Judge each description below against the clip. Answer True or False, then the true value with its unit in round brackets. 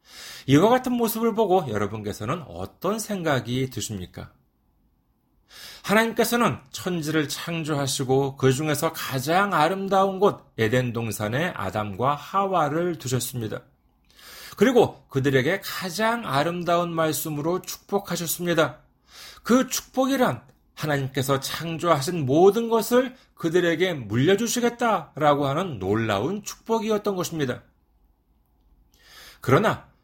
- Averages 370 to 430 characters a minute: False (270 characters per minute)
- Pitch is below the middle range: False (160 Hz)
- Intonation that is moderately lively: False (7.3 semitones)